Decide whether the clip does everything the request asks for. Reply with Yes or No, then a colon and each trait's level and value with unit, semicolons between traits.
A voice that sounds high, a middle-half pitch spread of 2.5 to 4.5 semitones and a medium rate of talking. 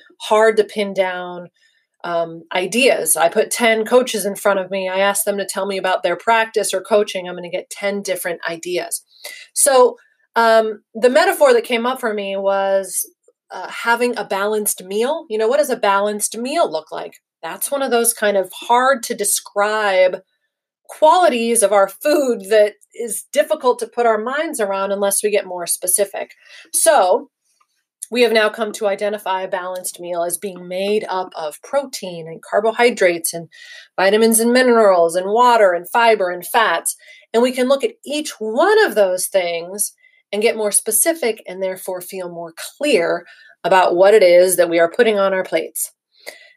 Yes: high, 210 Hz; average, 4.2 semitones; average, 180 wpm